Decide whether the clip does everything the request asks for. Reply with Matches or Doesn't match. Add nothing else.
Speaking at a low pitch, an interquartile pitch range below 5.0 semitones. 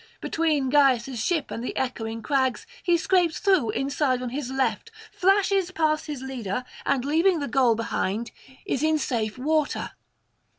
Doesn't match